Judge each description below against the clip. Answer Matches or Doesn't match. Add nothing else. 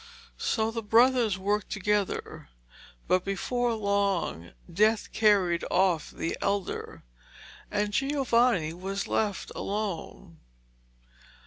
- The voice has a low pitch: Doesn't match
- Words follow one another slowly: Matches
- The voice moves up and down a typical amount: Matches